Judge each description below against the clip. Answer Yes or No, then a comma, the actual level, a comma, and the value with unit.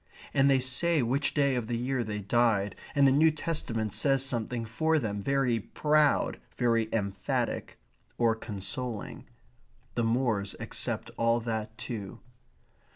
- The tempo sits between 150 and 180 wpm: No, average, 140 wpm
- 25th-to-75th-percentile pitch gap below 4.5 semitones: Yes, average, 3.6 semitones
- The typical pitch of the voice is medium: No, low, 120 Hz